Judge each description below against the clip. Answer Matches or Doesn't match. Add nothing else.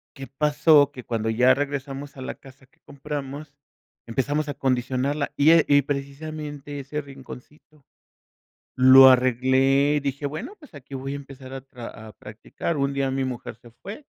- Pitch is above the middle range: Doesn't match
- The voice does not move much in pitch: Matches